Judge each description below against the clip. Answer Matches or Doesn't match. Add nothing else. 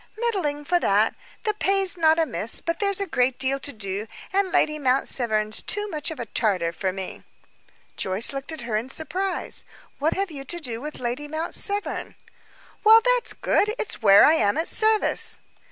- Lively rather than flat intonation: Matches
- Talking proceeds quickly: Doesn't match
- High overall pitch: Matches